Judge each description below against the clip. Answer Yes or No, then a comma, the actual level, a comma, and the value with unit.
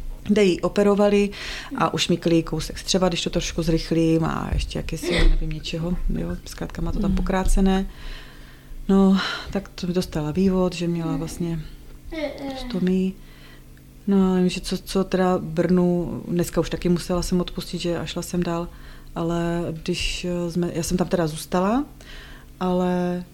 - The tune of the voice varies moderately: No, narrow, 2.1 semitones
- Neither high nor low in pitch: Yes, medium, 175 Hz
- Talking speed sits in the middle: Yes, average, 155 wpm